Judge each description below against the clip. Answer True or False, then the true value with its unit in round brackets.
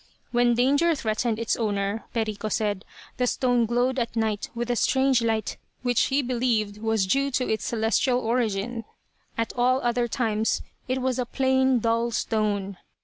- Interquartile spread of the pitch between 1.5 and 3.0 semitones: True (2.4 semitones)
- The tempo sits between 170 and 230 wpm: False (160 wpm)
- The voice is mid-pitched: False (235 Hz)